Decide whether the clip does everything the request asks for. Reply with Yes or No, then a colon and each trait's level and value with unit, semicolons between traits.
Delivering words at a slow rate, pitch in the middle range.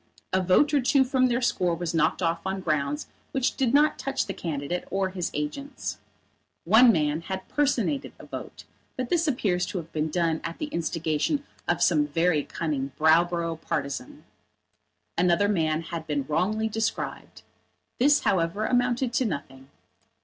No: average, 160 wpm; medium, 180 Hz